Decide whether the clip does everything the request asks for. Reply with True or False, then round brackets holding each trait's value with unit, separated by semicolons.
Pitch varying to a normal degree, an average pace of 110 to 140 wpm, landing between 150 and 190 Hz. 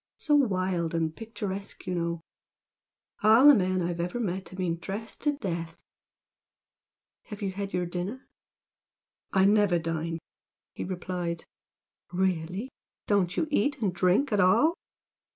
True (3.3 semitones; 135 wpm; 185 Hz)